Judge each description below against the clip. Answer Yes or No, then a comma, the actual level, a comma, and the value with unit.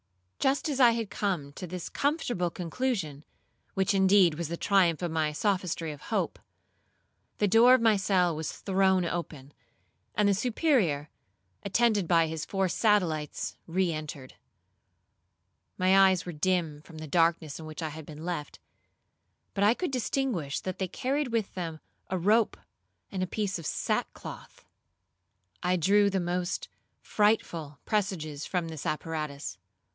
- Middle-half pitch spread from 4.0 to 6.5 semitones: Yes, average, 4.4 semitones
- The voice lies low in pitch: No, medium, 180 Hz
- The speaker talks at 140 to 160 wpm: Yes, average, 150 wpm